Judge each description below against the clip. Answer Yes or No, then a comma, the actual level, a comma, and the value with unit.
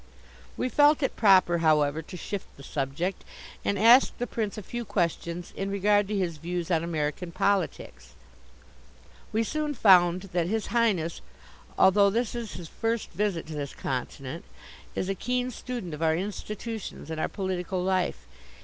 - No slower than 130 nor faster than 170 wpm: Yes, average, 160 wpm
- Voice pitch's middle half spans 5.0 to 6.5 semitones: No, average, 4.5 semitones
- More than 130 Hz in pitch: Yes, medium, 185 Hz